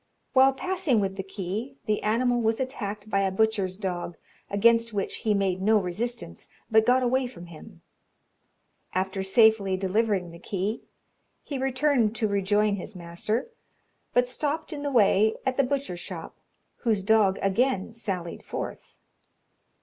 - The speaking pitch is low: No, high, 215 Hz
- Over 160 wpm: No, average, 150 wpm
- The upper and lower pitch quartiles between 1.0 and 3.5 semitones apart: No, average, 4.3 semitones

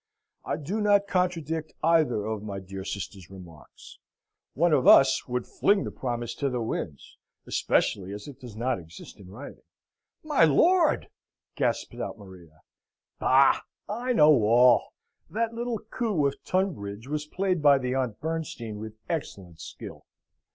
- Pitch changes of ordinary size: No, wide, 8.6 semitones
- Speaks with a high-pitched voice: No, low, 135 Hz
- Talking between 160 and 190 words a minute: No, average, 150 wpm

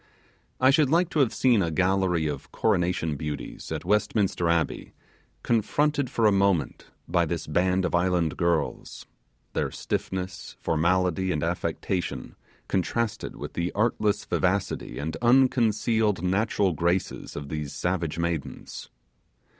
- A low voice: Yes, very low, 90 Hz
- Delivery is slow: Yes, slow, 130 wpm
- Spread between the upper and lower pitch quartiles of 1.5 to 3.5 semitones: No, average, 4.2 semitones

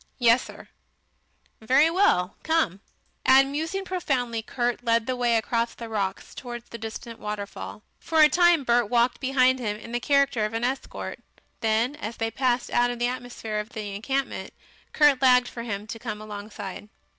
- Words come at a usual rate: Yes, average, 170 wpm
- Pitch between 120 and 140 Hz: No, high, 240 Hz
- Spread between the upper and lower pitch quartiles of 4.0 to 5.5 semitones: No, average, 3.1 semitones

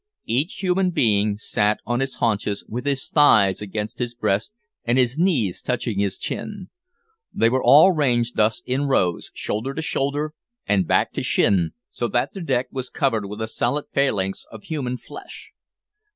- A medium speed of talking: Yes, average, 170 wpm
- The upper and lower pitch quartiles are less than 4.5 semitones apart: No, average, 5.0 semitones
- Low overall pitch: Yes, low, 120 Hz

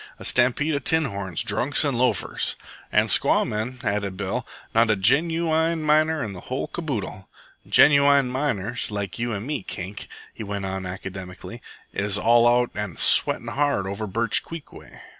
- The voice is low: Yes, low, 115 Hz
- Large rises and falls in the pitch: Yes, wide, 6.1 semitones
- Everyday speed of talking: Yes, average, 165 wpm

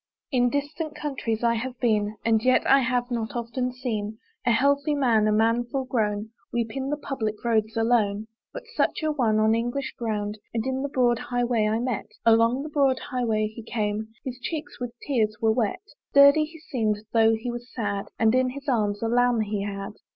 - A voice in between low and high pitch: No, high, 235 Hz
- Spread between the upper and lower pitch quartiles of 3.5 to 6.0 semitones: No, average, 3.1 semitones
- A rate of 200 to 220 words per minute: Yes, fast, 205 wpm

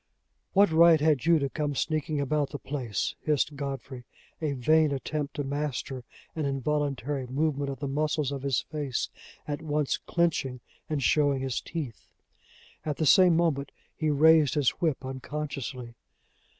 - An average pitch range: No, narrow, 2.3 semitones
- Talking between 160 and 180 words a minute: No, average, 150 wpm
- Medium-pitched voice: Yes, medium, 145 Hz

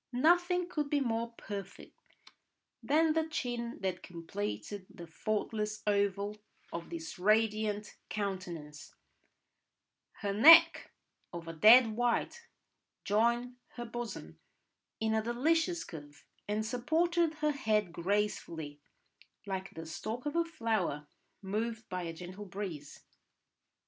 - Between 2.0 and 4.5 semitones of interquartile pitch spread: No, average, 5.1 semitones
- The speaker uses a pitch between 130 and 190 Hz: No, high, 215 Hz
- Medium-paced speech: No, slow, 115 wpm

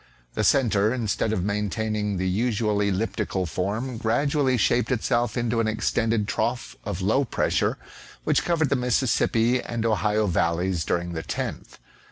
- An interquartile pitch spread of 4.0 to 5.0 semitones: No, average, 3.1 semitones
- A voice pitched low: Yes, low, 110 Hz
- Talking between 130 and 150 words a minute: Yes, average, 145 wpm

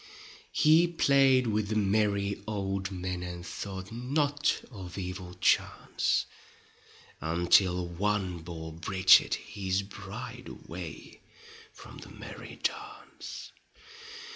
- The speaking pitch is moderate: No, low, 100 Hz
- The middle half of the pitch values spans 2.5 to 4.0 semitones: No, average, 4.4 semitones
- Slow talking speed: Yes, slow, 100 wpm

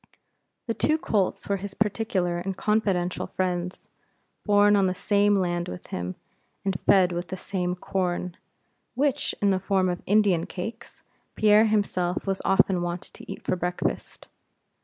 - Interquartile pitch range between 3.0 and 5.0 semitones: No, narrow, 2.5 semitones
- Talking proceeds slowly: No, average, 155 wpm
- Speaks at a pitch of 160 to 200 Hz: Yes, high, 190 Hz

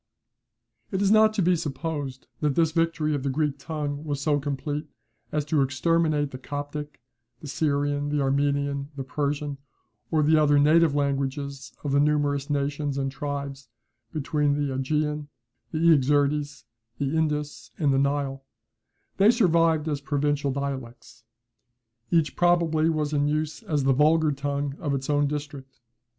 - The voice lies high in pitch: No, medium, 145 Hz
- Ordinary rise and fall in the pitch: No, narrow, 1.7 semitones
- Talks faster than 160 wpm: No, average, 150 wpm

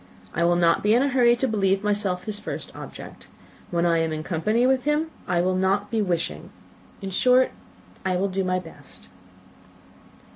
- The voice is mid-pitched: No, high, 195 Hz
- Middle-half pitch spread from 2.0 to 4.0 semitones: No, average, 4.7 semitones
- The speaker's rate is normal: Yes, average, 185 wpm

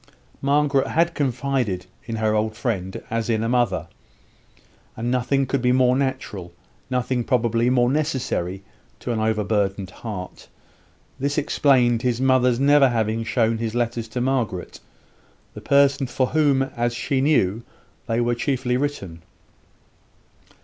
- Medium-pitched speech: No, low, 120 Hz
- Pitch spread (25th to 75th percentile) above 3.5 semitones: No, average, 3.2 semitones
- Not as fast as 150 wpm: Yes, slow, 135 wpm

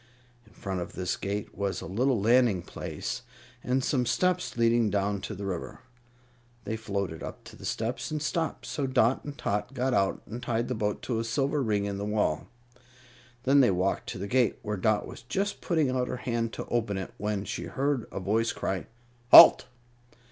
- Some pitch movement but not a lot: Yes, average, 4.2 semitones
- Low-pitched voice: Yes, low, 115 Hz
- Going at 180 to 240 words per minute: Yes, average, 200 wpm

